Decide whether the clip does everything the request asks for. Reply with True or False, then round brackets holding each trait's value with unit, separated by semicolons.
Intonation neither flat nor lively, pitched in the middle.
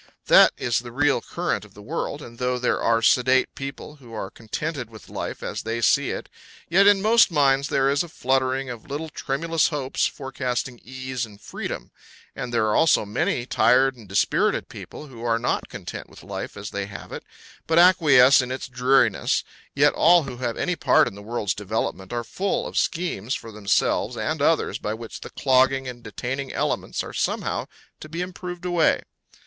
False (4.0 semitones; 130 Hz)